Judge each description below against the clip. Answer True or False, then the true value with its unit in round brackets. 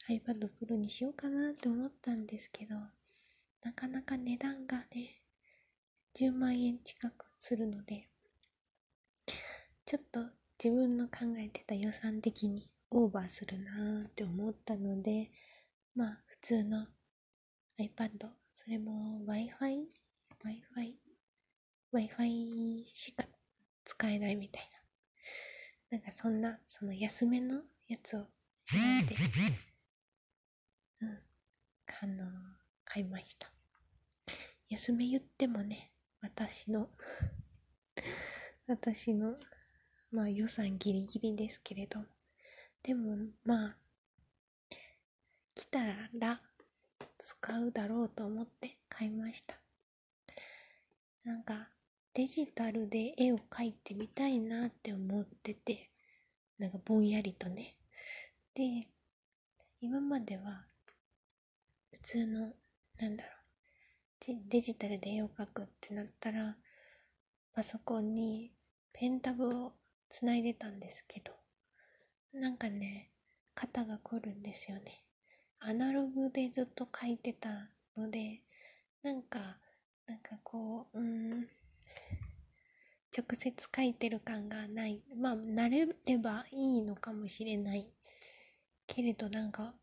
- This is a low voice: False (225 Hz)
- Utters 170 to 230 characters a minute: True (220 characters per minute)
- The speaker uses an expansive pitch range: False (2.6 semitones)